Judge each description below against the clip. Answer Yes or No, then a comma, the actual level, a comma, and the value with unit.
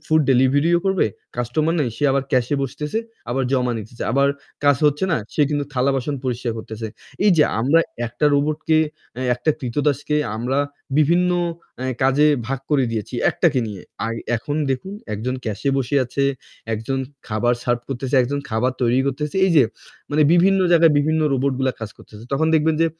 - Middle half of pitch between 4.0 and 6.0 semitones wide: No, average, 3.6 semitones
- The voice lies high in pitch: No, low, 135 Hz